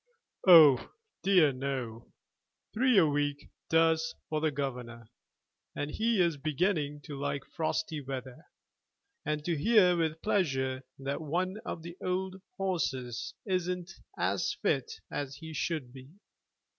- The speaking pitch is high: No, medium, 155 Hz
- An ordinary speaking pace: No, slow, 130 wpm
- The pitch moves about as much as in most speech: Yes, average, 4.6 semitones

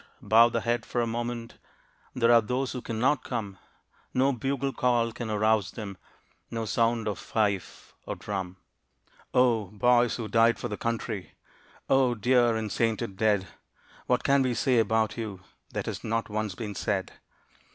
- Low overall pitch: Yes, low, 115 Hz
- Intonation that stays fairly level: Yes, narrow, 2.2 semitones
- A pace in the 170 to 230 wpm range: No, average, 160 wpm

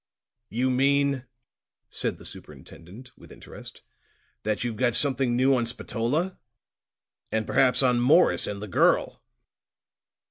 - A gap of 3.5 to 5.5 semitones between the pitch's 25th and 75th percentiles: No, average, 3.0 semitones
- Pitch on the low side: Yes, low, 125 Hz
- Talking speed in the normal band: No, slow, 120 wpm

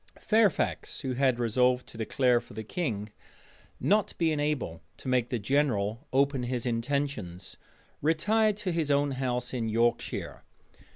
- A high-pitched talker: No, low, 130 Hz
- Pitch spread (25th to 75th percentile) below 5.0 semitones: Yes, average, 4.0 semitones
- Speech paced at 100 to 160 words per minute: Yes, average, 140 wpm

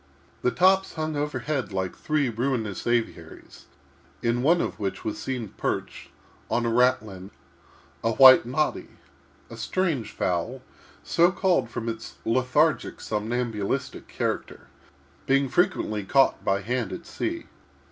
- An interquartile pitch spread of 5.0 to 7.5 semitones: Yes, average, 5.3 semitones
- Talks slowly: Yes, slow, 125 wpm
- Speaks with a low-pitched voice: Yes, low, 125 Hz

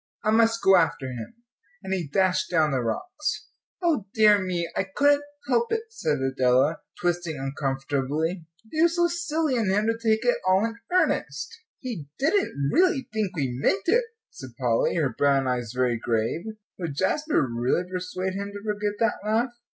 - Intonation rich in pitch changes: Yes, wide, 8.7 semitones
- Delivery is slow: No, average, 175 wpm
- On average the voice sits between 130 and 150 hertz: No, medium, 185 Hz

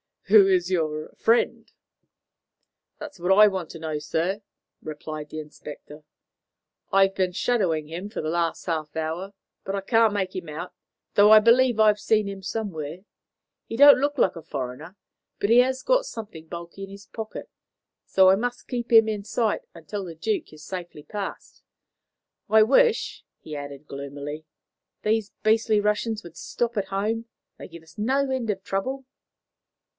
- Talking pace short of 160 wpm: No, average, 165 wpm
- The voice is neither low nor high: No, high, 195 Hz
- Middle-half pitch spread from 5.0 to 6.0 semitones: Yes, wide, 5.4 semitones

